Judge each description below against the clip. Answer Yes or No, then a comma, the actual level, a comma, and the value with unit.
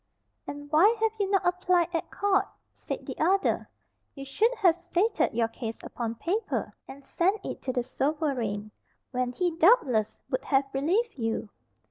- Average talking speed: Yes, average, 160 wpm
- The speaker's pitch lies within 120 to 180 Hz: No, very high, 320 Hz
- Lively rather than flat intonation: Yes, wide, 7.4 semitones